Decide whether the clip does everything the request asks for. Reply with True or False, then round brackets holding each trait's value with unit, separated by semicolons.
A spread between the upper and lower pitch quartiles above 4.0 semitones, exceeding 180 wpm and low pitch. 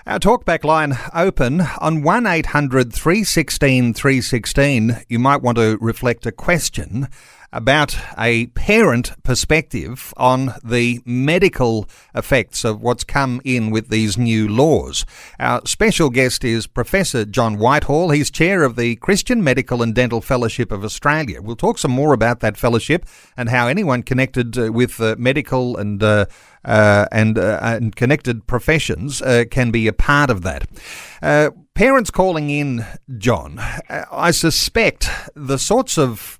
False (4.4 semitones; 160 wpm; 125 Hz)